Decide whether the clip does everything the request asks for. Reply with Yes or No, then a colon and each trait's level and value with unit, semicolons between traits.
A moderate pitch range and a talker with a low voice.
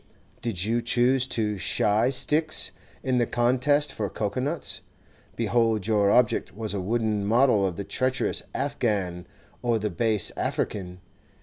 Yes: average, 3.6 semitones; low, 115 Hz